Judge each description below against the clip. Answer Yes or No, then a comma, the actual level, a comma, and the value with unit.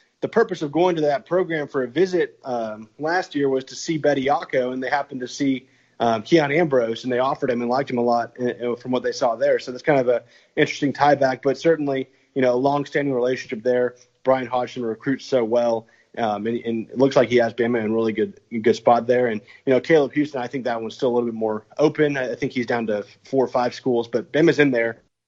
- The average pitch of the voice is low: Yes, low, 125 Hz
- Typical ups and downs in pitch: Yes, average, 3.1 semitones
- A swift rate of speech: Yes, fast, 255 wpm